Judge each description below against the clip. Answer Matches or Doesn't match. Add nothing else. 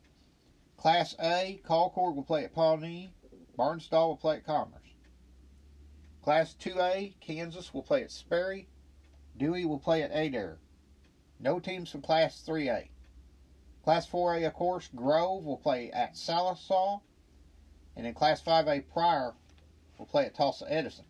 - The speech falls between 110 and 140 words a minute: Matches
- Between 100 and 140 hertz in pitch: Doesn't match